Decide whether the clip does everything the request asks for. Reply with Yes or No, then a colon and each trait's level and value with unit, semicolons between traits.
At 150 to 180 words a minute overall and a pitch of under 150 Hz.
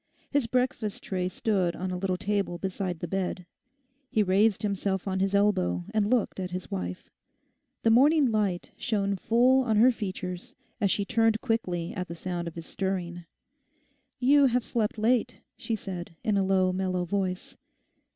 No: average, 165 wpm; high, 195 Hz